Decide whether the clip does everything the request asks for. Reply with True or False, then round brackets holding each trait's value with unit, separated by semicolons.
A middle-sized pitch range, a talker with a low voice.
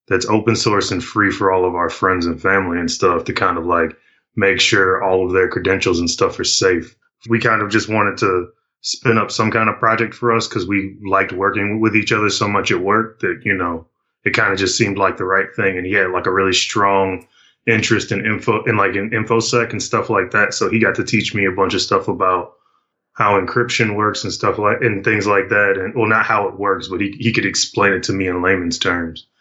True (3.3 semitones; 100 Hz)